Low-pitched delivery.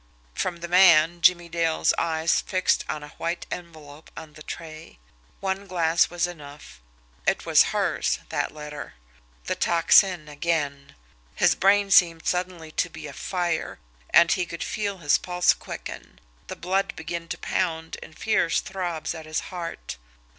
No: medium, 170 Hz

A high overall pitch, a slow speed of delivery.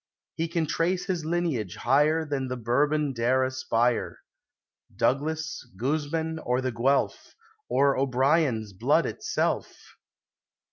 No: medium, 140 Hz; slow, 120 wpm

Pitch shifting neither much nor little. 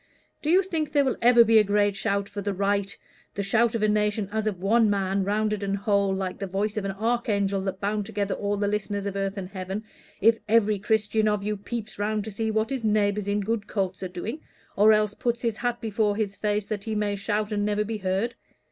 No: narrow, 1.6 semitones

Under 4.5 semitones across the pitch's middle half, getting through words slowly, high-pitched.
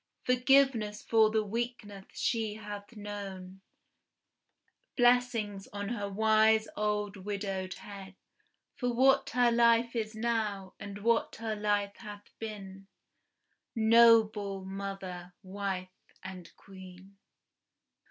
Yes: narrow, 2.6 semitones; slow, 105 wpm; high, 210 Hz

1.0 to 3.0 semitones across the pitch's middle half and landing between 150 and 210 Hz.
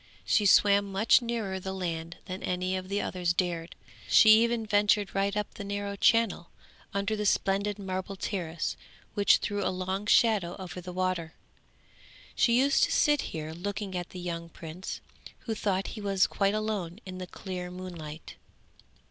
Yes: narrow, 2.4 semitones; high, 190 Hz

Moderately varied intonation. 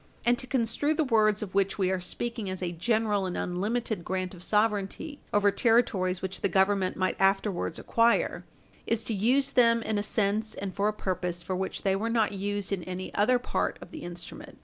Yes: average, 3.3 semitones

